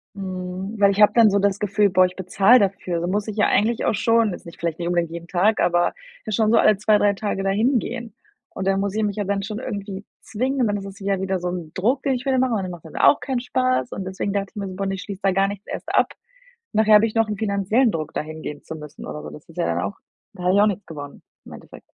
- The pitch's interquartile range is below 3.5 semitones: Yes, average, 2.7 semitones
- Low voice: No, high, 200 Hz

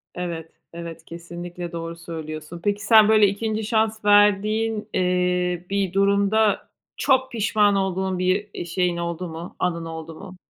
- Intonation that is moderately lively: Yes, average, 3.4 semitones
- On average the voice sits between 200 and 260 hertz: No, medium, 185 Hz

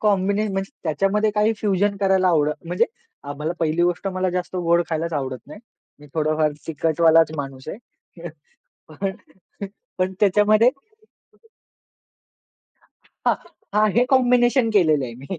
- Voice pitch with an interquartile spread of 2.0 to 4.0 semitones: No, average, 4.7 semitones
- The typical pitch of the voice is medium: Yes, medium, 180 Hz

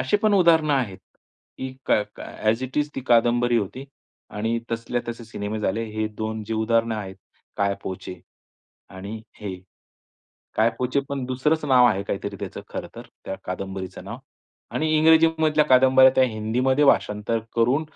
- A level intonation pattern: No, average, 3.7 semitones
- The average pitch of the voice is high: No, low, 115 Hz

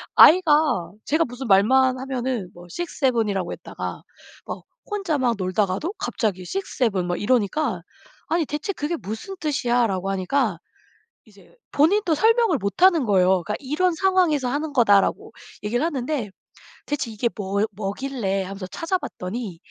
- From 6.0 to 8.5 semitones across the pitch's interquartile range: Yes, wide, 7.6 semitones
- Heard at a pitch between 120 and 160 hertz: No, high, 245 Hz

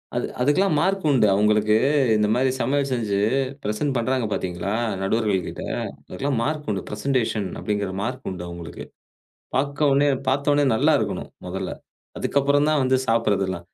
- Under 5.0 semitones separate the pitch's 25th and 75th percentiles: No, wide, 5.4 semitones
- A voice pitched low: Yes, low, 120 Hz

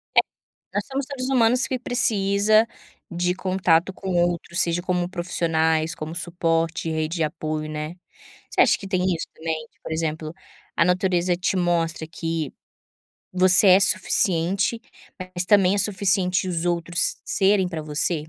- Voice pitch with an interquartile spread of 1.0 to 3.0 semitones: Yes, average, 2.7 semitones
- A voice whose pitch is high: No, medium, 175 Hz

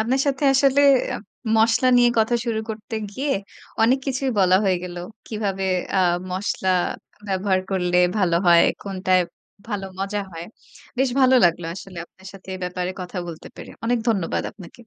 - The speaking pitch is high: Yes, high, 195 Hz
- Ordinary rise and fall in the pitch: Yes, average, 4.4 semitones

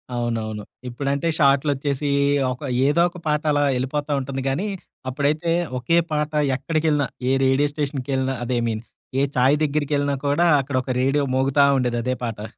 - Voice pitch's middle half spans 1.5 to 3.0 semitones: Yes, narrow, 2.4 semitones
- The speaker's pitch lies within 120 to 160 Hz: Yes, medium, 140 Hz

